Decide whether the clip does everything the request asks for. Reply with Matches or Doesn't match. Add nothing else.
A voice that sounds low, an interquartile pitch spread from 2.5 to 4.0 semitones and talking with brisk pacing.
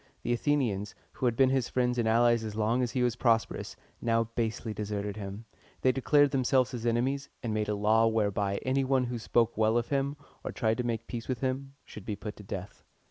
Matches